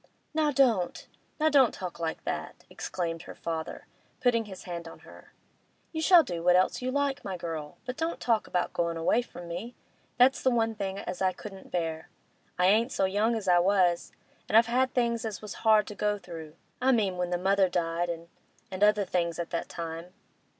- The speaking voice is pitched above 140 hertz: Yes, high, 190 Hz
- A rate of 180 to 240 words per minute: Yes, average, 195 wpm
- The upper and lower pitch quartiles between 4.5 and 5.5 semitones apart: Yes, average, 5.1 semitones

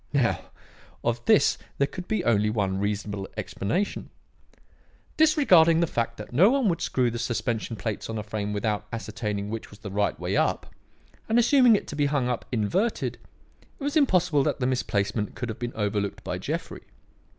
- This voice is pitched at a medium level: No, low, 120 Hz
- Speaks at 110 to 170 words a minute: No, average, 180 wpm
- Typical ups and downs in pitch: No, wide, 8.3 semitones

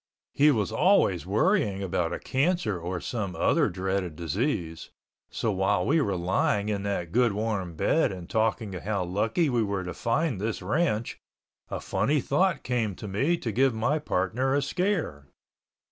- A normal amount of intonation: No, wide, 6.2 semitones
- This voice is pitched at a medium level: No, low, 105 Hz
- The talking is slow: No, average, 165 wpm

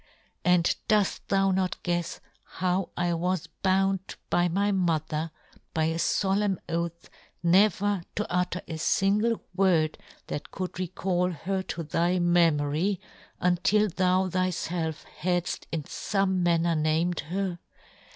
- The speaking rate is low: Yes, slow, 130 wpm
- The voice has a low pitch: No, medium, 180 Hz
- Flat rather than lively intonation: Yes, narrow, 2.3 semitones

